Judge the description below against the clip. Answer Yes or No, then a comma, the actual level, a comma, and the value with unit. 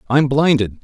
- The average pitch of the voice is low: Yes, low, 130 Hz